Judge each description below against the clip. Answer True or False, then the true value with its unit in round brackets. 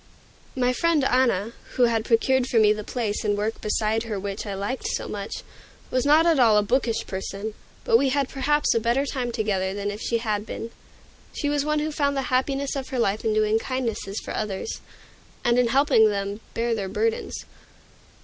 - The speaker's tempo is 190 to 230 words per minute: True (200 wpm)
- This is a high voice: True (230 Hz)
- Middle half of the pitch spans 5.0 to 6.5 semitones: False (3.9 semitones)